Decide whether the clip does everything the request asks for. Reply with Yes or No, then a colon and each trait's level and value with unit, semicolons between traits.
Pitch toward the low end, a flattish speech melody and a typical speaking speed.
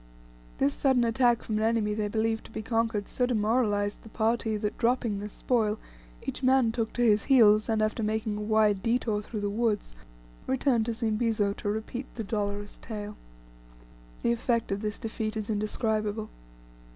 No: high, 220 Hz; narrow, 1.9 semitones; average, 175 wpm